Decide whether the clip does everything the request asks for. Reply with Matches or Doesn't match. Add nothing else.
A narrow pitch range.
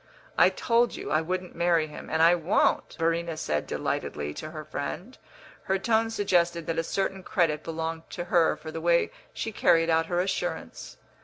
Matches